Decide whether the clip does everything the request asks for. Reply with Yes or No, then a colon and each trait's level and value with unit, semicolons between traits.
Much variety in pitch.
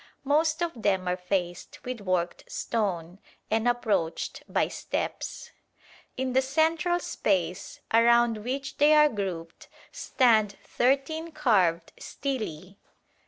Yes: wide, 7.0 semitones